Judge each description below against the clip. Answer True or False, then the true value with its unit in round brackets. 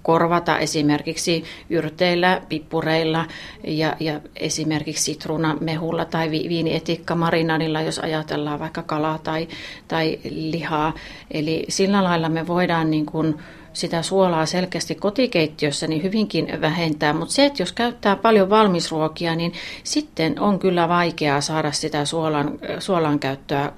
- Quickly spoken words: False (120 wpm)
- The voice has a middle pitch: True (160 Hz)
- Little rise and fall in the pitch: True (1.6 semitones)